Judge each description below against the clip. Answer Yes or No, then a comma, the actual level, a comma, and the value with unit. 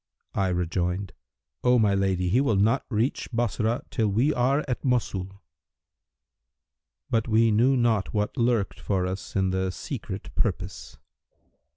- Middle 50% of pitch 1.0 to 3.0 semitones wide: No, average, 4.1 semitones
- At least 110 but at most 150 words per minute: Yes, average, 140 wpm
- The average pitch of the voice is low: Yes, low, 110 Hz